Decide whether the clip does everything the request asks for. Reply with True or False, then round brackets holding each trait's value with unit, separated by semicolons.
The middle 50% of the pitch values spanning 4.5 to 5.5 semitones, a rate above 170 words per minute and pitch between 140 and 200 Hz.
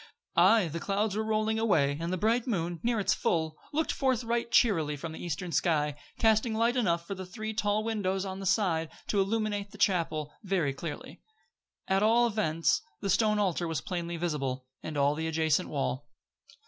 True (5.1 semitones; 185 wpm; 190 Hz)